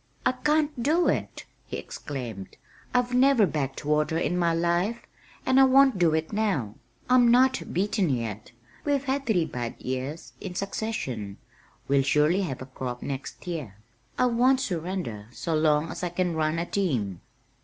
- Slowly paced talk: No, average, 165 wpm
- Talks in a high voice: No, medium, 170 Hz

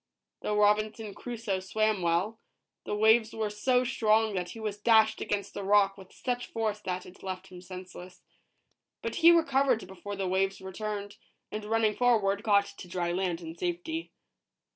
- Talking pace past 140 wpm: Yes, average, 165 wpm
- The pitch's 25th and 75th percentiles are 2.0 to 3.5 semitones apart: Yes, average, 2.8 semitones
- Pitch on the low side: No, high, 205 Hz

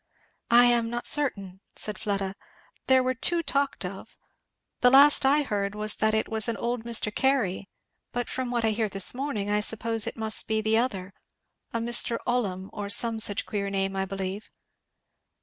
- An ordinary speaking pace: Yes, average, 185 wpm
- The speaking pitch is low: No, high, 220 Hz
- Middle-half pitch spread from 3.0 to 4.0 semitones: Yes, average, 3.4 semitones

